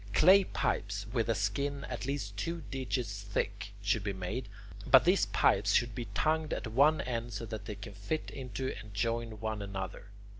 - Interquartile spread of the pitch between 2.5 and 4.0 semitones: No, average, 4.7 semitones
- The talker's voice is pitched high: No, low, 115 Hz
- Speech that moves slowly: No, average, 185 wpm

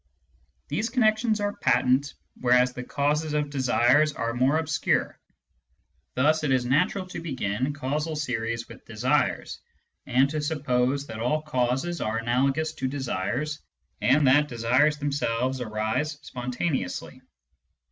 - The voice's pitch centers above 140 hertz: No, low, 135 Hz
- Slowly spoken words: Yes, slow, 125 wpm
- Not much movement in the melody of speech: No, average, 3.6 semitones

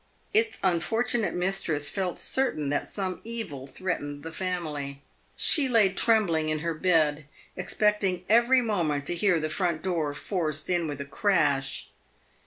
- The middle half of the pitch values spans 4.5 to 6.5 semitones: Yes, average, 4.9 semitones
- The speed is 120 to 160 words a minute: Yes, average, 145 wpm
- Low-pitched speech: No, medium, 175 Hz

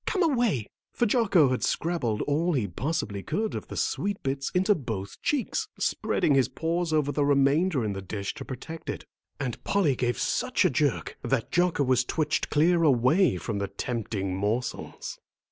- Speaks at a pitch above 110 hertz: Yes, medium, 140 Hz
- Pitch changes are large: Yes, wide, 6.7 semitones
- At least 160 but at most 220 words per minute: Yes, average, 175 wpm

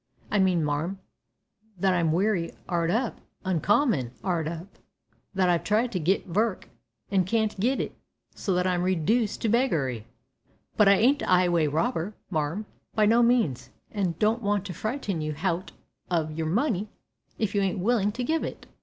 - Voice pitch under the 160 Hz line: No, high, 190 Hz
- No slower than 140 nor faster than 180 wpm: Yes, average, 170 wpm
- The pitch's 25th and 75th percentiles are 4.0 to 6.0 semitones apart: Yes, average, 4.4 semitones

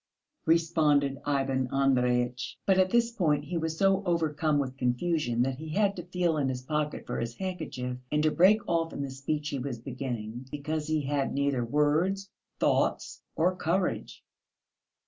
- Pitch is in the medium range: Yes, medium, 150 Hz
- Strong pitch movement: No, average, 4.1 semitones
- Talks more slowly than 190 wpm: Yes, average, 165 wpm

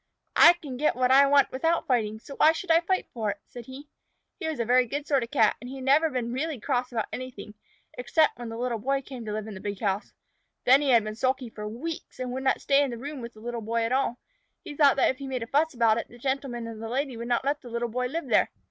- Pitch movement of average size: Yes, average, 3.2 semitones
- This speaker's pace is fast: Yes, fast, 280 wpm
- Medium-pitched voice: No, very high, 255 Hz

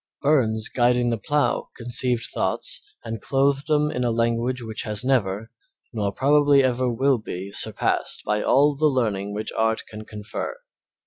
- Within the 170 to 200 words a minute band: No, average, 155 wpm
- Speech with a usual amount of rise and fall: Yes, average, 3.9 semitones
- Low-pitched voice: Yes, low, 120 Hz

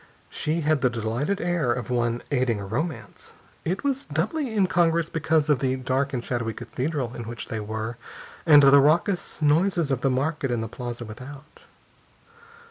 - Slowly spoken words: No, average, 170 wpm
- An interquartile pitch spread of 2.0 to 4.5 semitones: No, average, 5.2 semitones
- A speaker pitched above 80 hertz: Yes, medium, 140 Hz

